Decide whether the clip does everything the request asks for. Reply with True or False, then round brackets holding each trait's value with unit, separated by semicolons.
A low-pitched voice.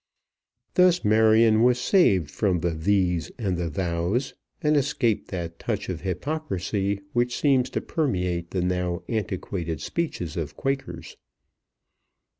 True (100 Hz)